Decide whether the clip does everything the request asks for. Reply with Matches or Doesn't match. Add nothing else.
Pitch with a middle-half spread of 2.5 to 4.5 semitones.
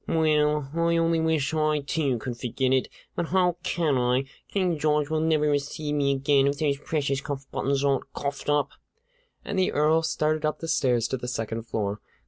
Matches